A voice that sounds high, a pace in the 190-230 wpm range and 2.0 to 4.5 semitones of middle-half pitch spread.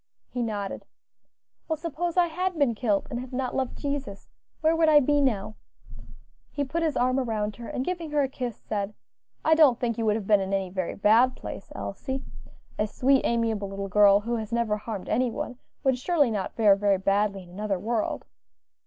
No: high, 235 Hz; average, 200 wpm; average, 4.9 semitones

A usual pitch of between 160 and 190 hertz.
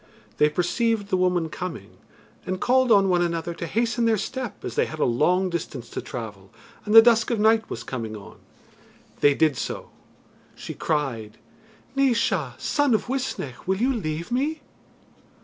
Yes: medium, 185 Hz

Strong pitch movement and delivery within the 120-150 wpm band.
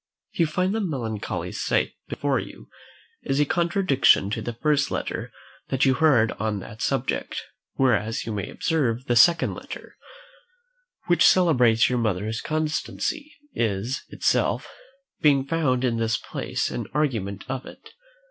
Yes: wide, 5.8 semitones; average, 140 wpm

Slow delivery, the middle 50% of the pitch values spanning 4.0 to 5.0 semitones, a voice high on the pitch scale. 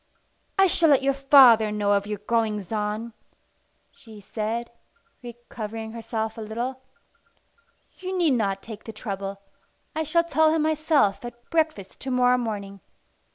No: average, 145 wpm; average, 4.6 semitones; high, 230 Hz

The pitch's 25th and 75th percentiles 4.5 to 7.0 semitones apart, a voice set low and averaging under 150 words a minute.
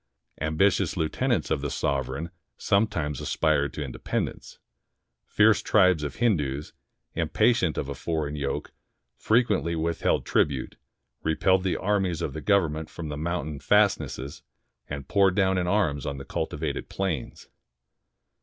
Yes: average, 5.0 semitones; very low, 80 Hz; slow, 135 wpm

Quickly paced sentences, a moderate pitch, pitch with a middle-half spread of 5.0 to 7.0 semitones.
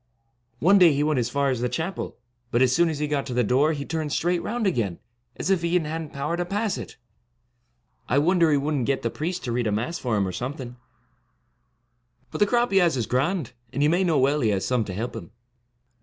Yes: fast, 245 wpm; medium, 145 Hz; wide, 5.6 semitones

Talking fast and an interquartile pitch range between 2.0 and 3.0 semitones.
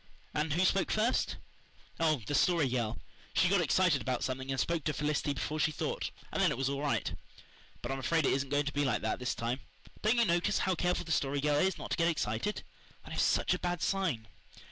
No: fast, 230 wpm; average, 4.6 semitones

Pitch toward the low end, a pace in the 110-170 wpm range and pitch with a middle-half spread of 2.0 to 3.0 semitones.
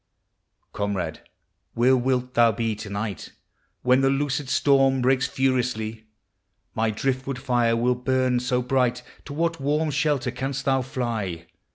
Yes: low, 125 Hz; average, 140 wpm; narrow, 2.5 semitones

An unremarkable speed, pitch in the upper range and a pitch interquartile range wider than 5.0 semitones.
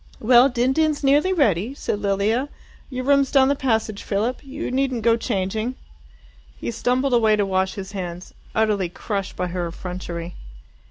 Yes: average, 160 wpm; high, 220 Hz; wide, 5.5 semitones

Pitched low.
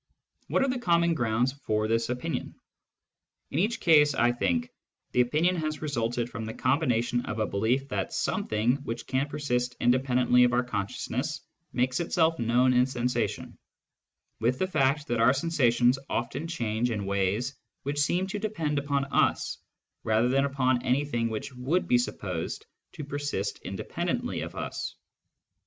Yes: low, 125 Hz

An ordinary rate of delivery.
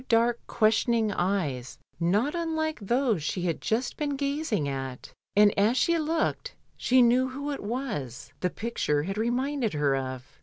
Yes: average, 160 wpm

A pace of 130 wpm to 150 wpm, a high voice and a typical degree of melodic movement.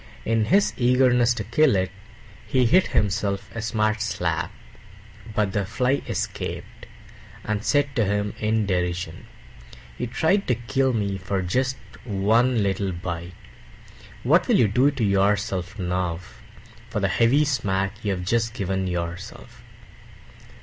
No: average, 140 wpm; low, 105 Hz; average, 4.1 semitones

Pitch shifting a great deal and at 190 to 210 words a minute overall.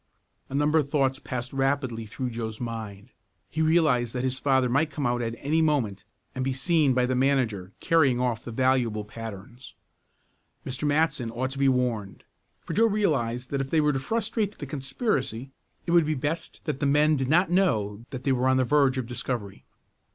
No: average, 3.6 semitones; average, 195 wpm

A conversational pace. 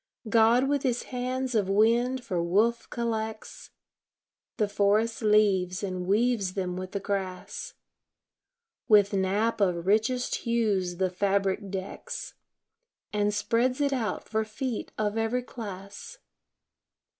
No: slow, 120 wpm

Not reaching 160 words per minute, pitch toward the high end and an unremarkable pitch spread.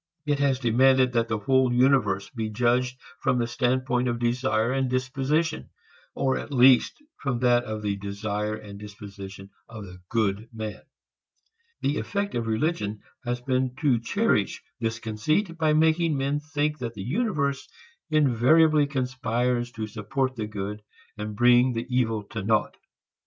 No: average, 150 wpm; low, 125 Hz; average, 3.8 semitones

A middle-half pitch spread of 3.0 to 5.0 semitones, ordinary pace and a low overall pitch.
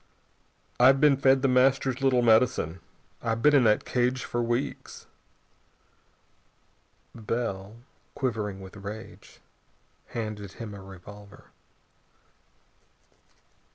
No: average, 3.9 semitones; slow, 95 wpm; low, 115 Hz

